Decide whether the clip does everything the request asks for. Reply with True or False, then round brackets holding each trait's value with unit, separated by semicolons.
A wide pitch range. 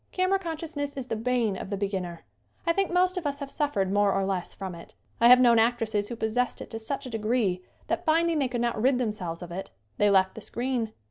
True (5.8 semitones)